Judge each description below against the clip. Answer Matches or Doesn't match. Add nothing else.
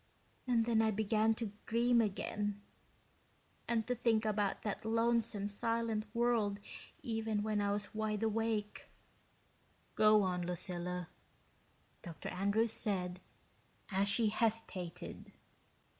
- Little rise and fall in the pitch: Matches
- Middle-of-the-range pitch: Doesn't match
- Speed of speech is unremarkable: Doesn't match